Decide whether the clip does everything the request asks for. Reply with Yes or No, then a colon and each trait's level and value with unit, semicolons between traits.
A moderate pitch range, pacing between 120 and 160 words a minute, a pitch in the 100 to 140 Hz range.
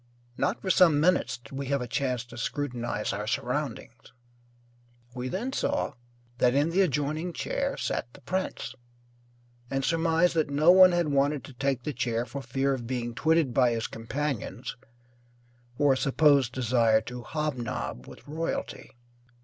Yes: average, 4.2 semitones; average, 155 wpm; low, 135 Hz